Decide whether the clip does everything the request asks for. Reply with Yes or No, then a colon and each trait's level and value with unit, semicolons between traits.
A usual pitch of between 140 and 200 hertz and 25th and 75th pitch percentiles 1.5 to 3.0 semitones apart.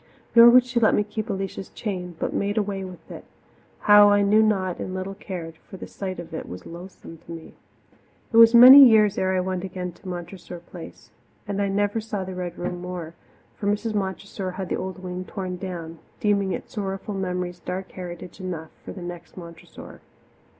Yes: high, 190 Hz; narrow, 2.4 semitones